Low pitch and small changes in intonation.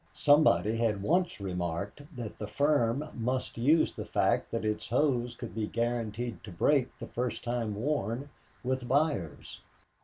No: low, 120 Hz; average, 4.6 semitones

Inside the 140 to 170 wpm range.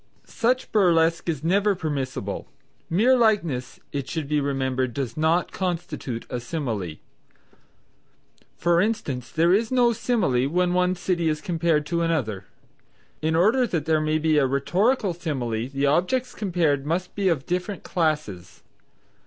Yes: average, 145 wpm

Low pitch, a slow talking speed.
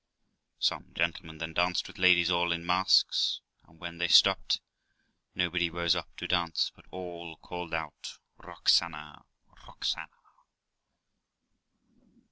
Yes: very low, 85 Hz; slow, 115 wpm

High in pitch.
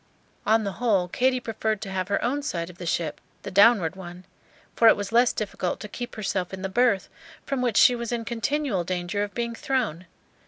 Yes: high, 210 Hz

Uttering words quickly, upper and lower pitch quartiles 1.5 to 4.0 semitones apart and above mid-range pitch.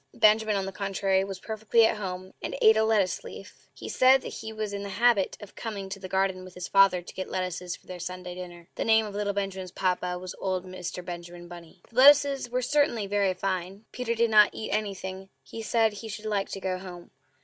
Yes: fast, 225 wpm; average, 2.9 semitones; high, 195 Hz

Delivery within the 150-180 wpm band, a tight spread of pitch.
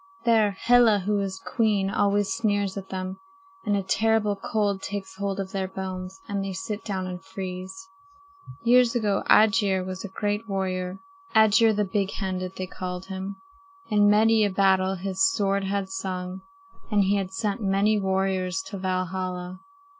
Yes: average, 160 wpm; narrow, 1.6 semitones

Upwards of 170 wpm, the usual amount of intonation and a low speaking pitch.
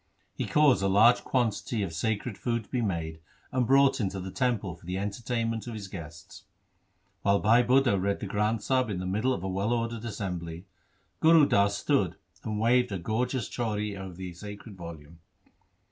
Yes: average, 185 wpm; average, 4.0 semitones; low, 105 Hz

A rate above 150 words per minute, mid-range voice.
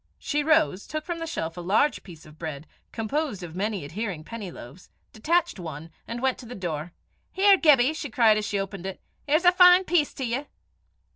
No: fast, 205 wpm; high, 225 Hz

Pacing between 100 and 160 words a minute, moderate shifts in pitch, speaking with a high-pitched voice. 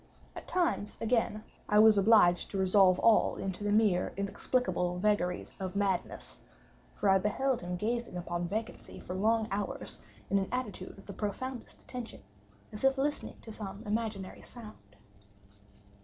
Yes: average, 150 wpm; average, 3.2 semitones; high, 205 Hz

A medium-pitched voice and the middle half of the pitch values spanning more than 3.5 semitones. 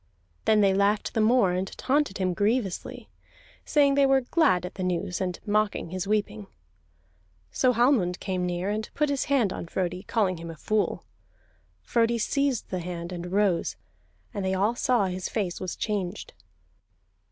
No: high, 200 Hz; average, 4.4 semitones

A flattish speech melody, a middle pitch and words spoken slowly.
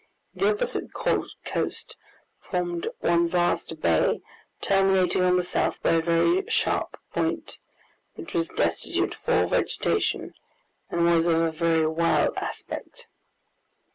Yes: narrow, 1.9 semitones; medium, 170 Hz; slow, 125 wpm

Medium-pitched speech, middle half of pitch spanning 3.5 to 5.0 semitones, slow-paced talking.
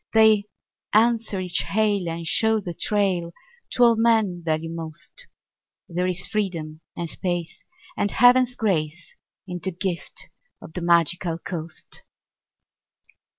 Yes: medium, 180 Hz; average, 4.2 semitones; slow, 125 wpm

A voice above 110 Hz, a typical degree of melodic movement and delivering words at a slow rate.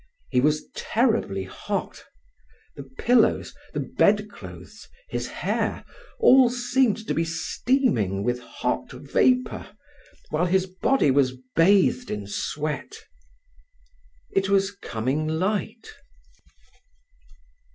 No: medium, 185 Hz; wide, 9.0 semitones; slow, 100 wpm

